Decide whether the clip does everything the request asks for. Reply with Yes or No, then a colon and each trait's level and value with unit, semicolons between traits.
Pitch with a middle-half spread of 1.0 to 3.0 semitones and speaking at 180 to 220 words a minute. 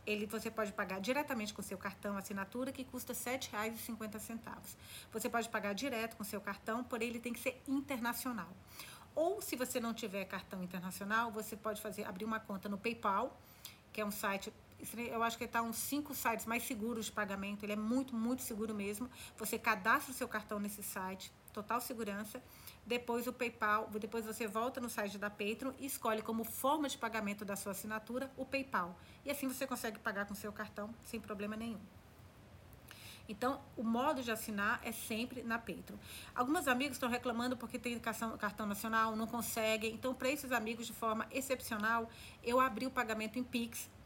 Yes: average, 2.7 semitones; fast, 185 wpm